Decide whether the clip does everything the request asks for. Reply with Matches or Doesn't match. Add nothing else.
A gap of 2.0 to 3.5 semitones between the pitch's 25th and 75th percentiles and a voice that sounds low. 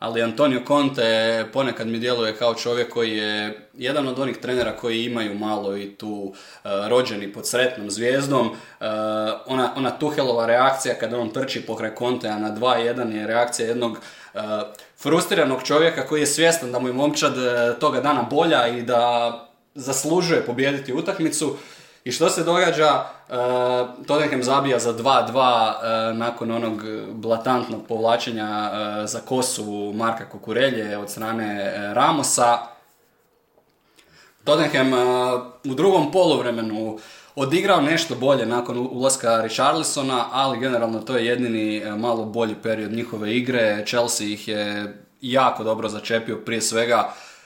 Matches